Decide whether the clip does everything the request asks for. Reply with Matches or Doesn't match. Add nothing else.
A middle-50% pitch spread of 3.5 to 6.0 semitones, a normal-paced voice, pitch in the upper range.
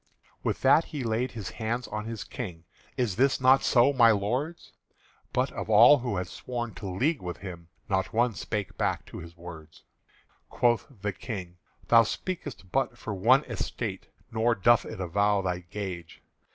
Doesn't match